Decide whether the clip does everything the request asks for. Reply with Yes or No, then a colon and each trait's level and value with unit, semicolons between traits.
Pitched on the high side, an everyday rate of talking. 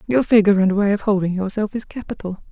No: high, 205 Hz; fast, 215 wpm